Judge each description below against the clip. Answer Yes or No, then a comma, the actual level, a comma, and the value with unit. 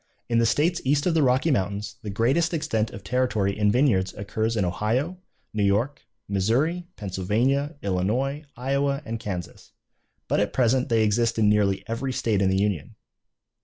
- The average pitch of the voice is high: No, low, 115 Hz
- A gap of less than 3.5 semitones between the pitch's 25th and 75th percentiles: No, average, 5.1 semitones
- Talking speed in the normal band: Yes, average, 165 wpm